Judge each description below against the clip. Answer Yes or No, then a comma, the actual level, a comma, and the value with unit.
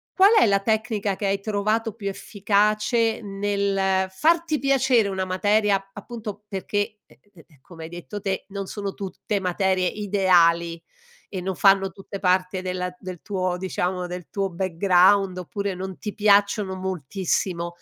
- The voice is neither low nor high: No, high, 195 Hz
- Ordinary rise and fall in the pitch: No, narrow, 2.0 semitones